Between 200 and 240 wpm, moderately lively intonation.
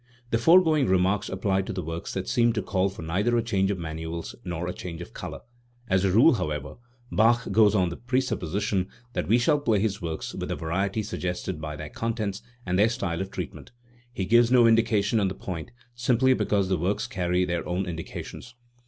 Yes: fast, 205 wpm; average, 4.3 semitones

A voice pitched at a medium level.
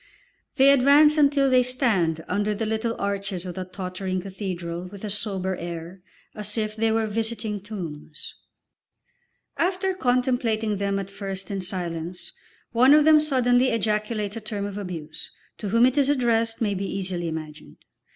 No: high, 210 Hz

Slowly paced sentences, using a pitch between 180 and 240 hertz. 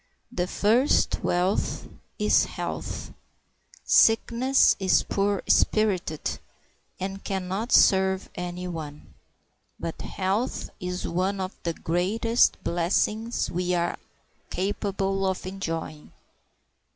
Yes: slow, 100 wpm; high, 190 Hz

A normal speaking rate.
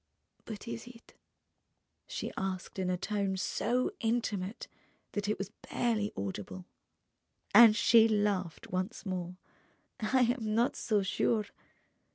No: slow, 125 wpm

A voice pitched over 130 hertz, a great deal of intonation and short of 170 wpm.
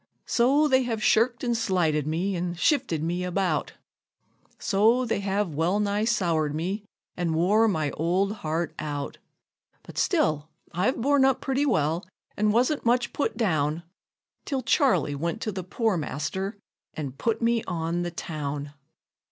Yes: high, 190 Hz; wide, 6.2 semitones; average, 150 wpm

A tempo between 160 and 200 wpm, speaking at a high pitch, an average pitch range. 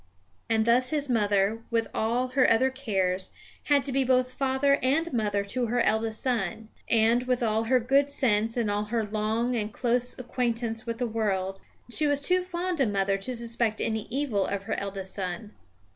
Yes: average, 190 wpm; high, 230 Hz; average, 3.3 semitones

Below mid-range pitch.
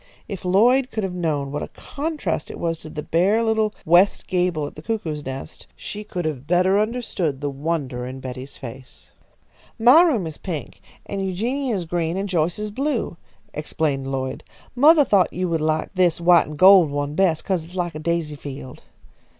No: medium, 175 Hz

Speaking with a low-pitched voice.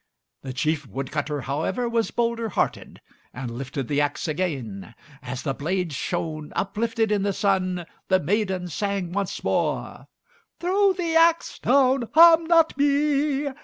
No: high, 190 Hz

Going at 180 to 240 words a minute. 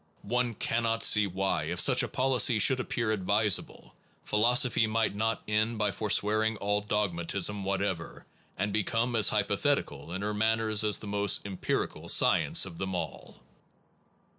No: average, 155 wpm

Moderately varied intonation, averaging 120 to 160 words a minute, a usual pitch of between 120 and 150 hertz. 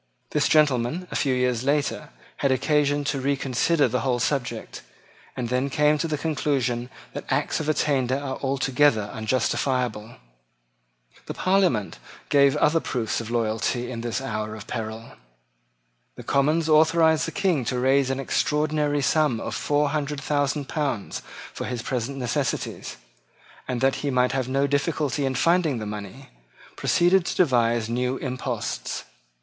Yes: average, 3.5 semitones; average, 150 wpm; low, 135 Hz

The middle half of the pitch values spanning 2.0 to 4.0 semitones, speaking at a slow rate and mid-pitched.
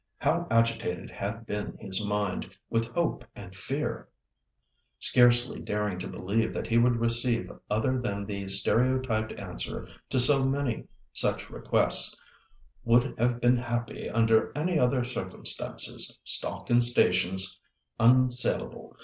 No: average, 3.1 semitones; slow, 125 wpm; low, 115 Hz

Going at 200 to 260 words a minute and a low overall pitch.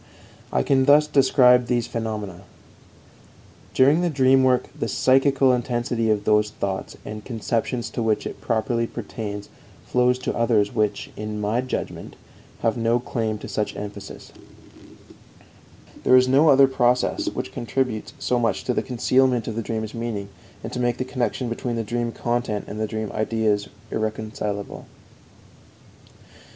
No: average, 145 wpm; low, 115 Hz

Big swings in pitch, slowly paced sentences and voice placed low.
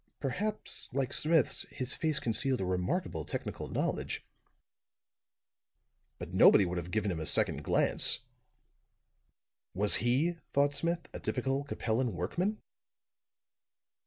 Yes: wide, 7.4 semitones; slow, 115 wpm; low, 130 Hz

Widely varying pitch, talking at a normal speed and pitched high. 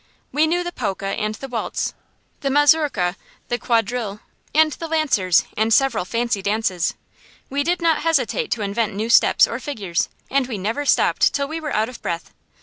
Yes: wide, 5.7 semitones; average, 180 wpm; high, 240 Hz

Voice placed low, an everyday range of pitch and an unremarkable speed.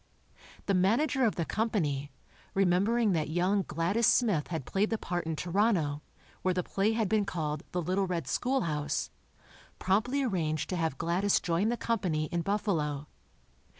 No: medium, 185 Hz; average, 4.7 semitones; average, 155 wpm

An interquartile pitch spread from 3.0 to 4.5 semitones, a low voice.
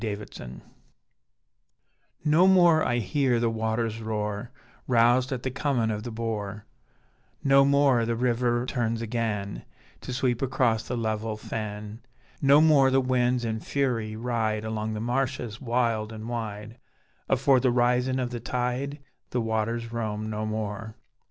No: narrow, 2.6 semitones; low, 115 Hz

